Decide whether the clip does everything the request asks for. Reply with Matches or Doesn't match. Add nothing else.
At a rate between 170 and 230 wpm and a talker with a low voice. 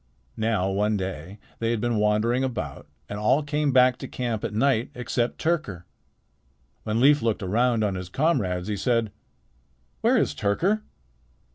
Doesn't match